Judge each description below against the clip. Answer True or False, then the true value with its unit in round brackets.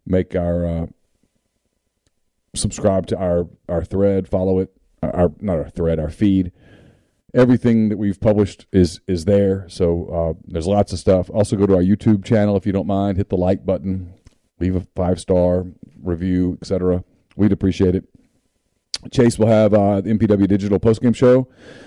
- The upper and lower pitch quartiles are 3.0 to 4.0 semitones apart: False (2.4 semitones)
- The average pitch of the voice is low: True (95 Hz)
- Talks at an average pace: True (170 wpm)